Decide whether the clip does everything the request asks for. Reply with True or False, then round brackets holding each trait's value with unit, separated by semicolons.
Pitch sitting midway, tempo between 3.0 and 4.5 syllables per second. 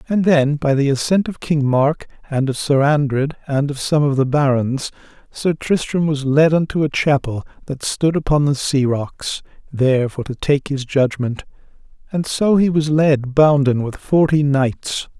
True (145 Hz; 4.4 syllables/s)